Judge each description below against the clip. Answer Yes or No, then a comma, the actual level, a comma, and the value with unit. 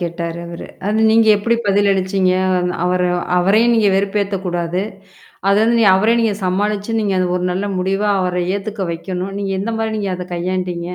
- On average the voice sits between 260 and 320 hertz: No, high, 195 Hz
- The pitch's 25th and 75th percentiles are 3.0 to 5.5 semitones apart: No, narrow, 2.4 semitones